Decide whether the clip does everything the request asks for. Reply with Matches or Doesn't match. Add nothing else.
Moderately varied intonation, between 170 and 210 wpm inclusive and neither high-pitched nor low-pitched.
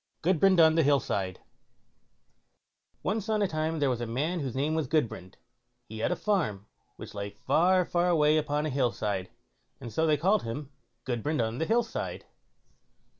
Doesn't match